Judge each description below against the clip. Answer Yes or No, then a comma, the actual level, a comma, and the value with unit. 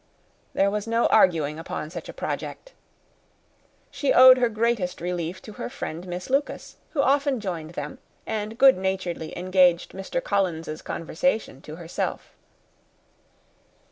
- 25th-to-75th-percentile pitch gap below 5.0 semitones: No, wide, 5.6 semitones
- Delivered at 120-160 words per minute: Yes, slow, 135 wpm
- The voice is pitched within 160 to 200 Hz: Yes, high, 190 Hz